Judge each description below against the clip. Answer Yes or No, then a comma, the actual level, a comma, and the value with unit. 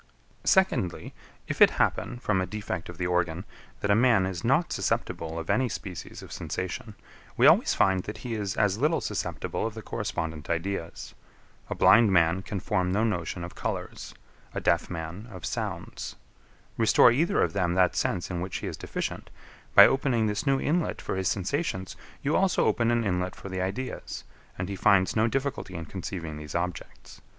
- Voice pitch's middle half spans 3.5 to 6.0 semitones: Yes, average, 4.5 semitones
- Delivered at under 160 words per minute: No, average, 185 wpm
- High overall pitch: No, very low, 95 Hz